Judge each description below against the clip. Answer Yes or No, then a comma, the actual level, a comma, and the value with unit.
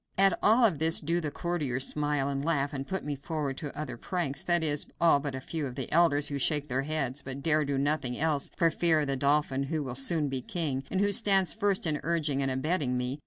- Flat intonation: No, average, 3.3 semitones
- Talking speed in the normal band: No, fast, 245 wpm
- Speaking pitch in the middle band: Yes, medium, 150 Hz